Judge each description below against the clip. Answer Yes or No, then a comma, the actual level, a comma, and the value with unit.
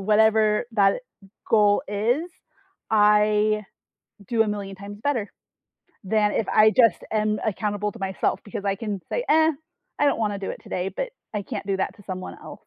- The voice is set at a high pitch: Yes, high, 210 Hz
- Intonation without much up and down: Yes, narrow, 1.6 semitones